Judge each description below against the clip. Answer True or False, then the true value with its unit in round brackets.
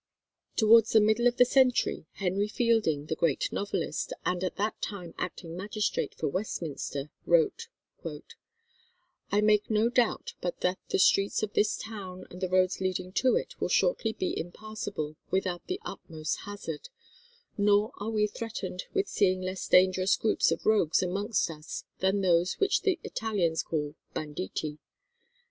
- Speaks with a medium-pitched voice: False (195 Hz)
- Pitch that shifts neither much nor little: True (3.6 semitones)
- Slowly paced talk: False (155 wpm)